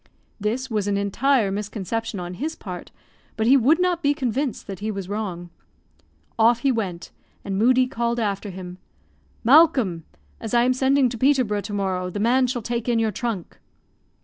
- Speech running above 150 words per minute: Yes, average, 175 wpm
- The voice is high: Yes, high, 225 Hz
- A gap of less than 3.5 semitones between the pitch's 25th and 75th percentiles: No, average, 4.4 semitones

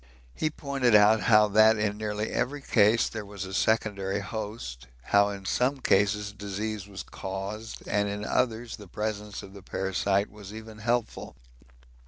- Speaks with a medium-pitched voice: No, low, 105 Hz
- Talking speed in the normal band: Yes, average, 160 wpm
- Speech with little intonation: Yes, narrow, 1.7 semitones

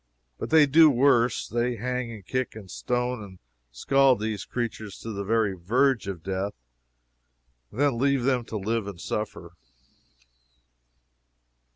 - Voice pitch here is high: No, low, 115 Hz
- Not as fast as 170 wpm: Yes, average, 150 wpm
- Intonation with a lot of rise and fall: No, average, 4.1 semitones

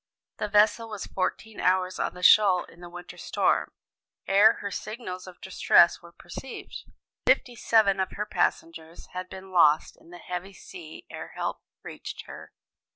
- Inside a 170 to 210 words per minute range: No, average, 160 wpm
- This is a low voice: No, medium, 185 Hz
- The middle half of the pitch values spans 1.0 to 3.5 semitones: Yes, average, 2.9 semitones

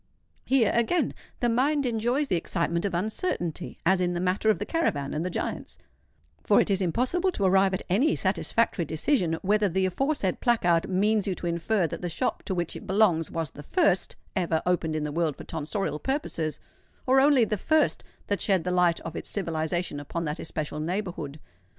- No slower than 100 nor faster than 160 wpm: No, average, 195 wpm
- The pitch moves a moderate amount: Yes, average, 4.8 semitones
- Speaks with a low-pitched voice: No, medium, 185 Hz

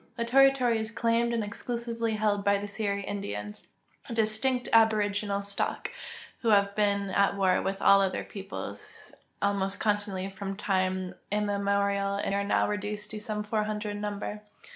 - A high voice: Yes, high, 205 Hz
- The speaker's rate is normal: Yes, average, 155 wpm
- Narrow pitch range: Yes, narrow, 1.5 semitones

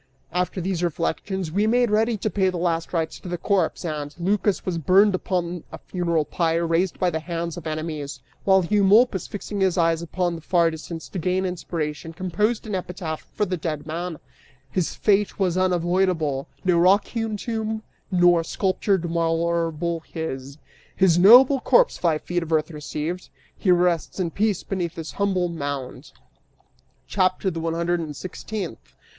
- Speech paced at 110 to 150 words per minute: No, average, 170 wpm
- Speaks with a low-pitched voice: No, medium, 175 Hz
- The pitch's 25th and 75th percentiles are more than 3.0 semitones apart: No, average, 2.7 semitones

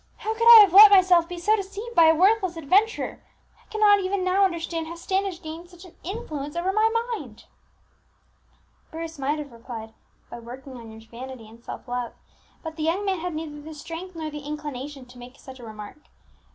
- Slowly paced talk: No, average, 200 wpm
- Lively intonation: Yes, wide, 6.1 semitones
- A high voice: Yes, very high, 325 Hz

